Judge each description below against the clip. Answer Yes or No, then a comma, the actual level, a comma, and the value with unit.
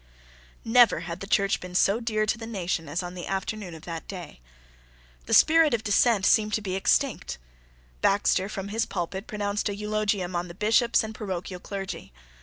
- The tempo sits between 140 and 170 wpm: No, average, 185 wpm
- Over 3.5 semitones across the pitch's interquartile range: No, average, 3.0 semitones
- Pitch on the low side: No, high, 200 Hz